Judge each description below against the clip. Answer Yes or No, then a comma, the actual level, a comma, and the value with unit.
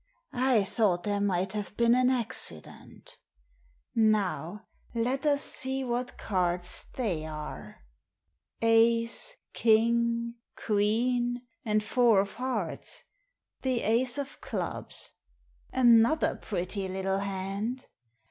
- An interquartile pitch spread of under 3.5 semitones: No, average, 3.8 semitones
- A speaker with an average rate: No, slow, 105 wpm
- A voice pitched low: No, high, 225 Hz